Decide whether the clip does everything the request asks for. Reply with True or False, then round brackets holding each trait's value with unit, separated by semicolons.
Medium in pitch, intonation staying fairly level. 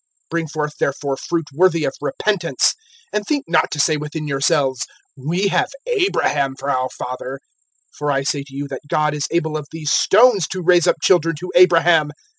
False (155 Hz; 3.7 semitones)